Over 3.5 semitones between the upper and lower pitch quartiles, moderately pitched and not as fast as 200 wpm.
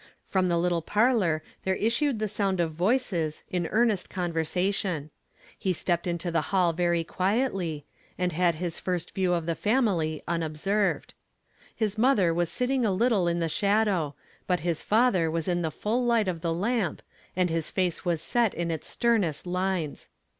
Yes: average, 3.9 semitones; medium, 180 Hz; average, 175 wpm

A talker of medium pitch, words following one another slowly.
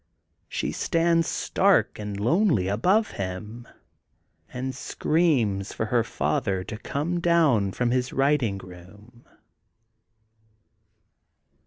No: low, 120 Hz; slow, 100 wpm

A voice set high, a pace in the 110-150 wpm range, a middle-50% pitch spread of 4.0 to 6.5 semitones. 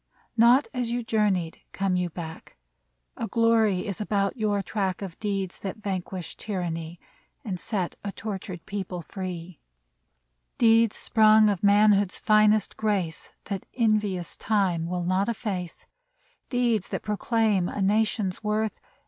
No: high, 200 Hz; average, 140 wpm; average, 2.9 semitones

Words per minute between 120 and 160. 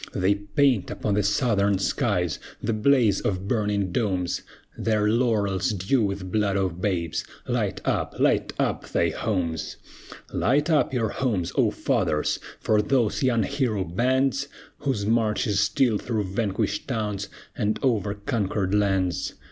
Yes: average, 140 wpm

